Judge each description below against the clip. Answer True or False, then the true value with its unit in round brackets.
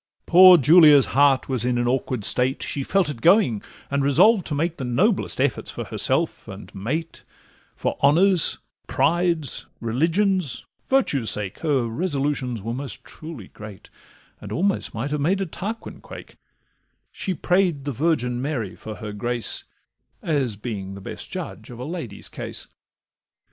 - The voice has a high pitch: False (140 Hz)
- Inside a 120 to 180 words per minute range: True (155 wpm)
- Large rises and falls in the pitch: True (5.9 semitones)